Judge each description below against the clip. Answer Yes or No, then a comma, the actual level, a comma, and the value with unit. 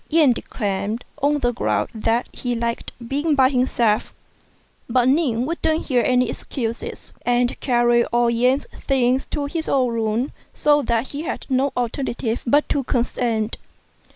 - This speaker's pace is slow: No, average, 150 wpm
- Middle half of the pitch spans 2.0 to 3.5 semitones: Yes, average, 2.8 semitones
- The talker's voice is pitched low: No, very high, 250 Hz